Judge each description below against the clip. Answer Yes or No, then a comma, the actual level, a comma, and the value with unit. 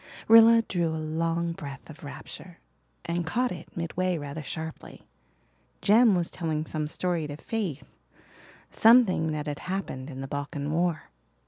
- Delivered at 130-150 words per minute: Yes, average, 145 wpm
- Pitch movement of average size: Yes, average, 3.3 semitones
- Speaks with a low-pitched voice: No, medium, 165 Hz